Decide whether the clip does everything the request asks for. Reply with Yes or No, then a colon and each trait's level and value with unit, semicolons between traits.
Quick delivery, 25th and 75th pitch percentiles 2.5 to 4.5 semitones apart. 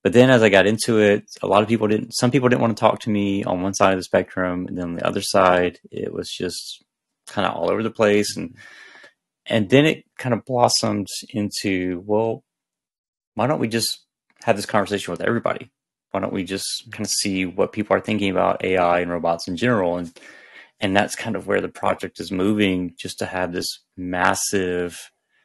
Yes: fast, 215 wpm; average, 3.2 semitones